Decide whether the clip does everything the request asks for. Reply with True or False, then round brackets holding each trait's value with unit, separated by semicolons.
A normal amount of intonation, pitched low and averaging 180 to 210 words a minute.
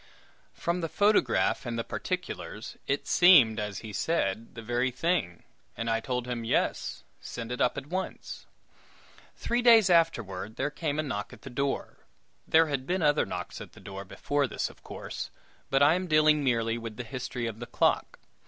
False (6.0 semitones; 130 Hz; 185 wpm)